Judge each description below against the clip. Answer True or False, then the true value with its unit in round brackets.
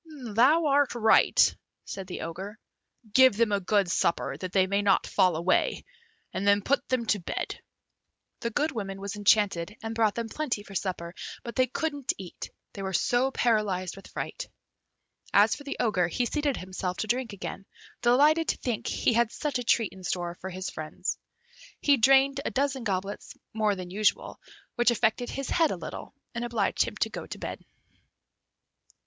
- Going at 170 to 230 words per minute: True (180 wpm)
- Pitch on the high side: True (215 Hz)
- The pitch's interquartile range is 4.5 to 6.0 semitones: True (4.9 semitones)